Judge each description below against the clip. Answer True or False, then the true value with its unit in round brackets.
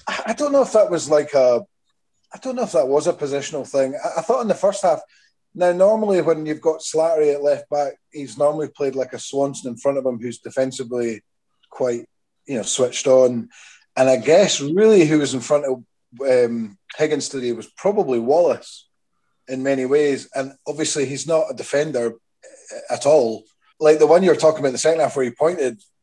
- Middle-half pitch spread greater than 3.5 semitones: True (4.1 semitones)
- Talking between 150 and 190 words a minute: False (205 wpm)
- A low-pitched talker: False (145 Hz)